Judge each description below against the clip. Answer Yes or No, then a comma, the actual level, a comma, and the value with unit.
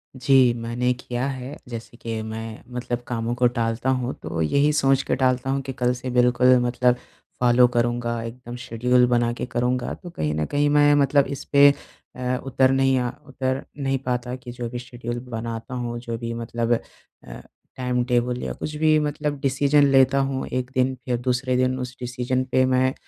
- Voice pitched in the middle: No, low, 125 Hz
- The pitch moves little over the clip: Yes, narrow, 1.7 semitones